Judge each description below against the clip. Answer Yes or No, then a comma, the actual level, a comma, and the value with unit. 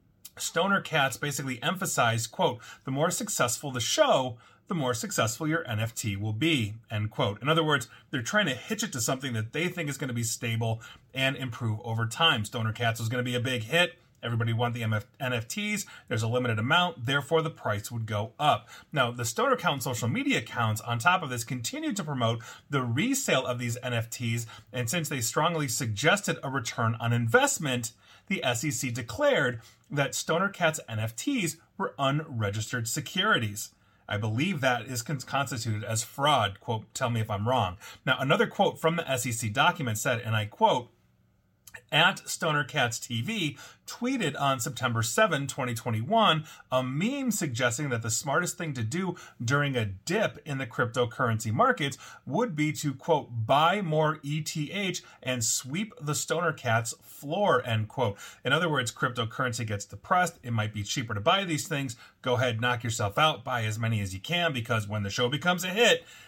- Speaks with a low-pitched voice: Yes, low, 125 Hz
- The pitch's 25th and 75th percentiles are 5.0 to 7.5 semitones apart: Yes, average, 5.3 semitones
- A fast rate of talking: No, average, 180 wpm